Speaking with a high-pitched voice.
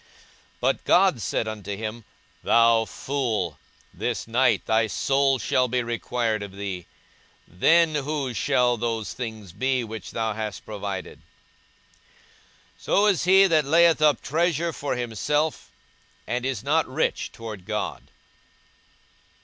No: low, 120 Hz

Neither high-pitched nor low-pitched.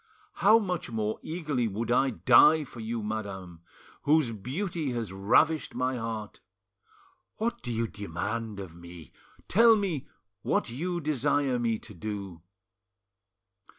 No: low, 120 Hz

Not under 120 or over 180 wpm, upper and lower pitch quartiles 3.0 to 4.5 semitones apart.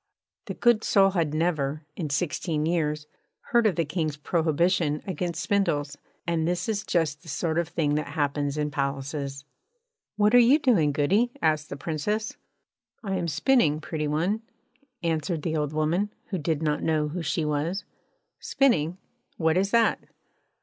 Yes: average, 160 wpm; average, 3.6 semitones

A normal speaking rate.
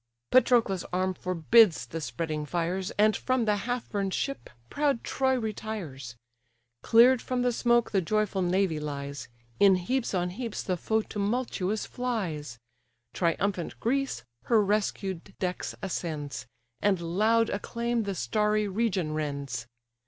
No: slow, 130 wpm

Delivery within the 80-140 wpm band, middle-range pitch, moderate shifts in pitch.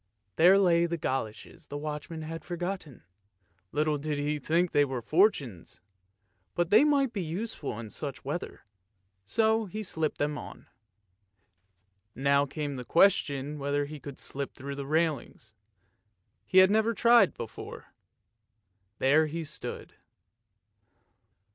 Yes: slow, 135 wpm; medium, 155 Hz; average, 4.1 semitones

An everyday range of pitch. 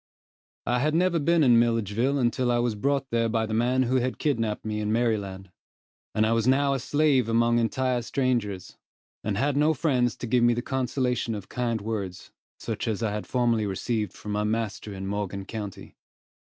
Yes: average, 3.3 semitones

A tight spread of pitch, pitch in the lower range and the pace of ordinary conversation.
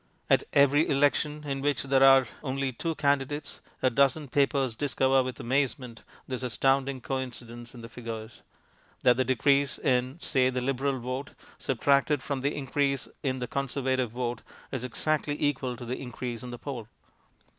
Yes: narrow, 2.1 semitones; low, 130 Hz; average, 160 wpm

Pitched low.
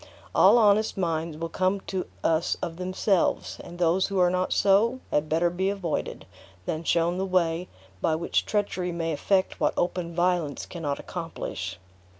No: medium, 175 Hz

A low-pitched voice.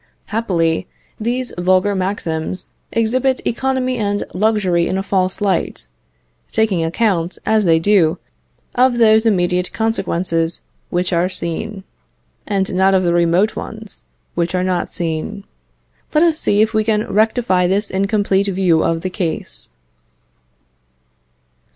No: high, 195 Hz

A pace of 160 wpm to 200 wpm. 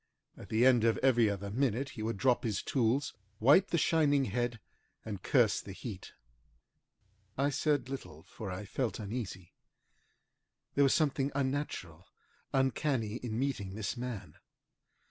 No: average, 145 wpm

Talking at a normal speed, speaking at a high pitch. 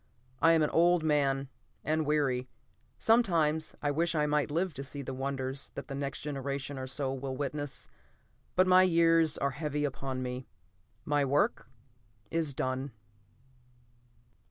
No: average, 150 wpm; medium, 145 Hz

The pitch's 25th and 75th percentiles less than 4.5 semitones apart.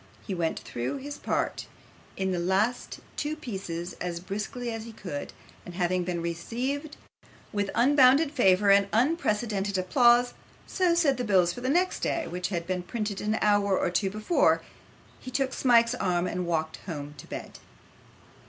No: wide, 5.6 semitones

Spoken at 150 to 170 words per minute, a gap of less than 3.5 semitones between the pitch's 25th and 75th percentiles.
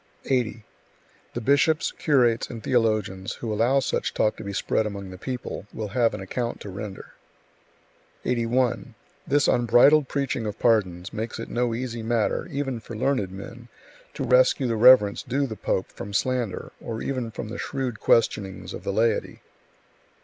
Yes: average, 165 wpm; average, 3.1 semitones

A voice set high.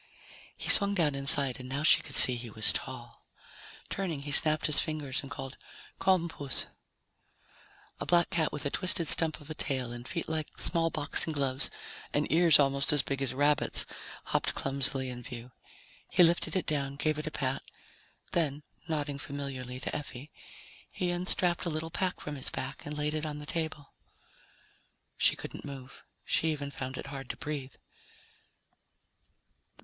No: medium, 145 Hz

